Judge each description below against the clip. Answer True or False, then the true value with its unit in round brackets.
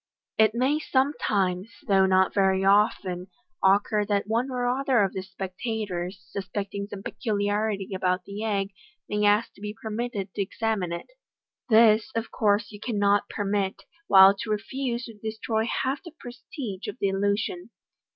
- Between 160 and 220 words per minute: False (150 wpm)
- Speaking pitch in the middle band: False (205 Hz)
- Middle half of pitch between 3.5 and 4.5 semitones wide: False (2.6 semitones)